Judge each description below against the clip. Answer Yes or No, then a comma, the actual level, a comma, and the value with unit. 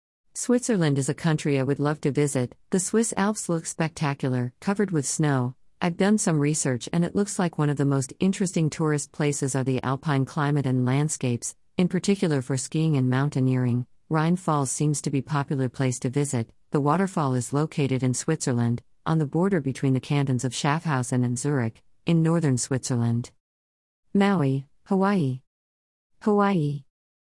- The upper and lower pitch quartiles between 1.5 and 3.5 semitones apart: No, average, 4.1 semitones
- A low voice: No, medium, 145 Hz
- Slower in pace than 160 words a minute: No, average, 170 wpm